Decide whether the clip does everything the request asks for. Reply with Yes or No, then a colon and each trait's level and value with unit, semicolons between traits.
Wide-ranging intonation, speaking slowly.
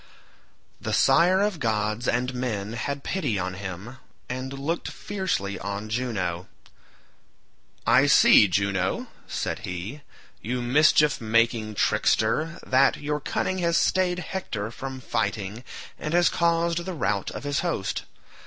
Yes: wide, 6.9 semitones; slow, 130 wpm